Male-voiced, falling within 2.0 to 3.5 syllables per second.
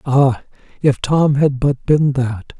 Yes: male; 3.3 syllables/s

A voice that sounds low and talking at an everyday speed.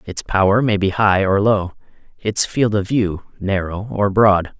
Yes: low, 100 Hz; average, 185 wpm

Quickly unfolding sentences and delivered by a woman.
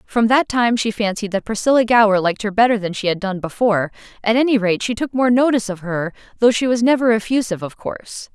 Yes: fast, 230 wpm; female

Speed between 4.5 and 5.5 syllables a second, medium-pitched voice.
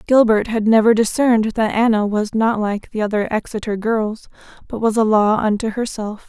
No: 5.1 syllables/s; high, 220 Hz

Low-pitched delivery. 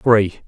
Yes: low, 105 Hz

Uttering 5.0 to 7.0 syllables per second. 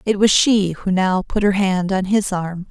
No: 4.2 syllables/s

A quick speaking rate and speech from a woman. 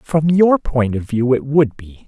No: fast, 230 wpm; male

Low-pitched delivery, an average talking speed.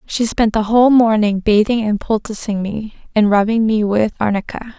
No: high, 215 Hz; average, 175 wpm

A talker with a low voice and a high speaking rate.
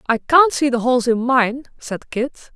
No: very high, 255 Hz; fast, 210 wpm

